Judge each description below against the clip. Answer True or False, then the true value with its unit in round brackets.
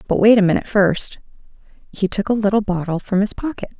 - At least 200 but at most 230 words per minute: True (205 wpm)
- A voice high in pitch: True (200 Hz)